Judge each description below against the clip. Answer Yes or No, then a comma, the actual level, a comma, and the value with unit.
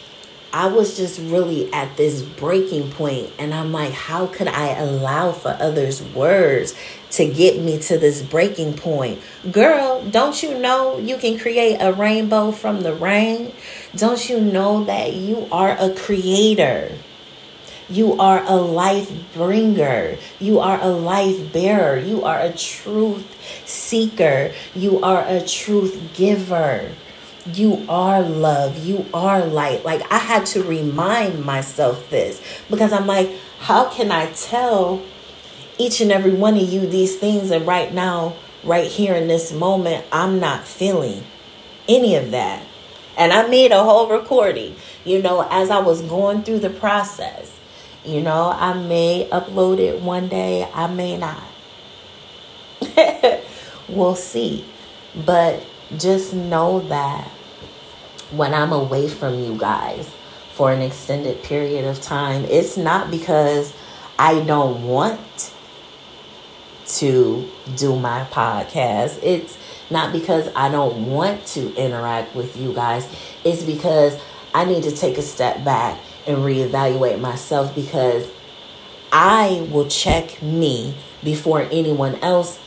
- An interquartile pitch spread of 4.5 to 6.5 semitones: Yes, average, 5.1 semitones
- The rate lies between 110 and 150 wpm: Yes, average, 140 wpm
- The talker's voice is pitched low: No, medium, 175 Hz